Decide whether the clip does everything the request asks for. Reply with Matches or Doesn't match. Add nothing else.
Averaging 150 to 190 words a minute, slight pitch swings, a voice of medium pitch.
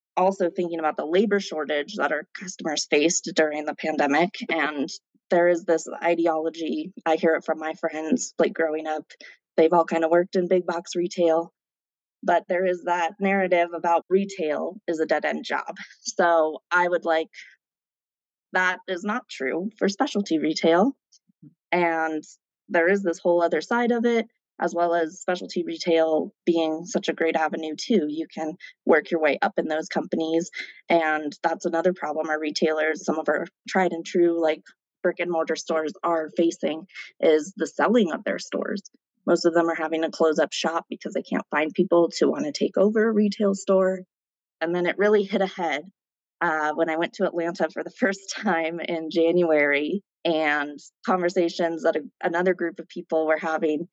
Matches